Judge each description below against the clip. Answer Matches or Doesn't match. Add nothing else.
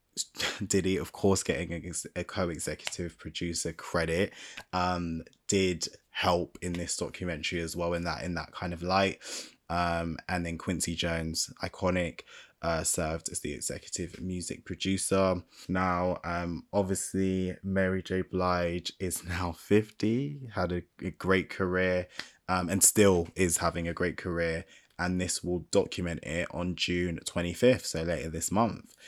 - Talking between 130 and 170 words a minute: Matches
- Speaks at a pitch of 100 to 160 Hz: Doesn't match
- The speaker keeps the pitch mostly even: Matches